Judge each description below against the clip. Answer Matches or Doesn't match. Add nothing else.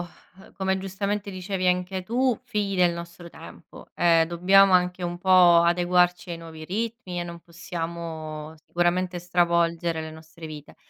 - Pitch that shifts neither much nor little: Doesn't match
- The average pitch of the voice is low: Doesn't match